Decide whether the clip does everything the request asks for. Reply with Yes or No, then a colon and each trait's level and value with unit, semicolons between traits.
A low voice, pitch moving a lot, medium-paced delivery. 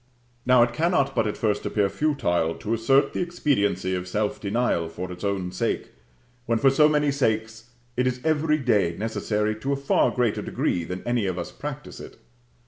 Yes: low, 115 Hz; wide, 5.7 semitones; average, 190 wpm